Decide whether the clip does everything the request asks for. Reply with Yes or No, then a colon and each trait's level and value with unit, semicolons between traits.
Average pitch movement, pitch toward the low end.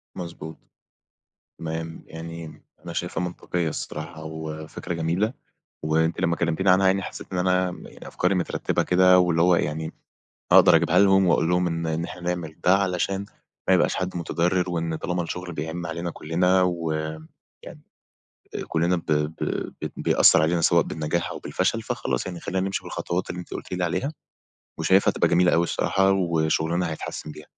No: narrow, 1.9 semitones; very low, 85 Hz